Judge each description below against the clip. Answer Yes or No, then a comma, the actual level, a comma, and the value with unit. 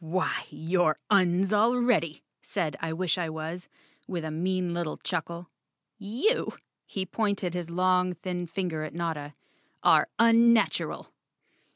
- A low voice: No, medium, 180 Hz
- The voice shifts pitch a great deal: No, average, 3.0 semitones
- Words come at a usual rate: No, slow, 130 wpm